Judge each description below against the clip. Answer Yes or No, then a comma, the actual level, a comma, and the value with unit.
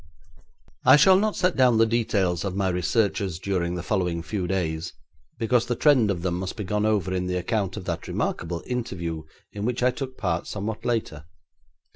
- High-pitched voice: No, low, 100 Hz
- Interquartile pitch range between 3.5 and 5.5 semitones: Yes, average, 4.7 semitones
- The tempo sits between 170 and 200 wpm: Yes, average, 190 wpm